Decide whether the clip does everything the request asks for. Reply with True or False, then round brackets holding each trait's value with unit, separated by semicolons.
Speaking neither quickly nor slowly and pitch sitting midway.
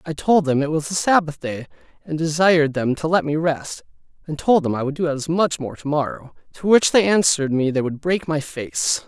False (230 wpm; 155 Hz)